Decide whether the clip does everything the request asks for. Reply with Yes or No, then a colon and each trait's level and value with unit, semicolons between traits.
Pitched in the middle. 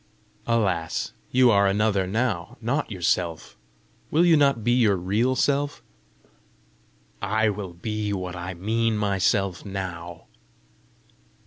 No: low, 105 Hz